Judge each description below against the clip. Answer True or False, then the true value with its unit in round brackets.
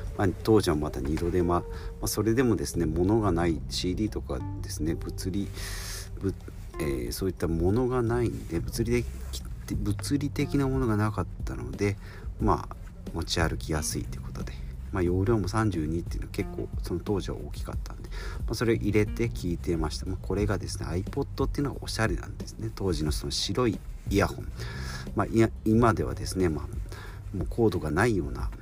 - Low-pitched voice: True (95 Hz)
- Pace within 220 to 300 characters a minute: False (380 characters per minute)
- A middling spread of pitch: True (3.9 semitones)